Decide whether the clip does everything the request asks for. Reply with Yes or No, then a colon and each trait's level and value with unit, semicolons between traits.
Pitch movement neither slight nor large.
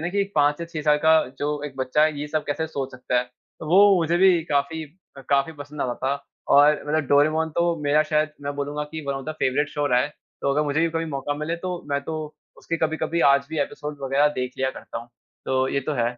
No: narrow, 2.2 semitones